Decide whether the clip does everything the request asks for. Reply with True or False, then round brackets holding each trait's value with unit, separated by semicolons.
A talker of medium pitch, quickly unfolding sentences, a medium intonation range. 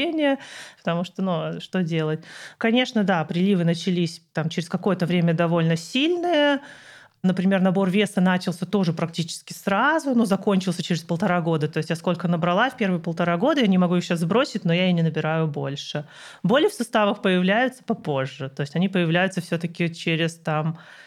True (180 Hz; 175 wpm; 3.5 semitones)